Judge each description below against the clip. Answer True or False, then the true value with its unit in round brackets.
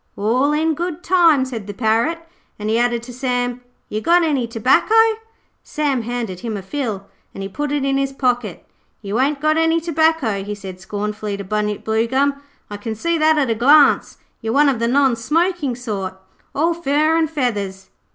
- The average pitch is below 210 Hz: False (250 Hz)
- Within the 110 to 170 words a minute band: False (190 wpm)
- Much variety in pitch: True (5.7 semitones)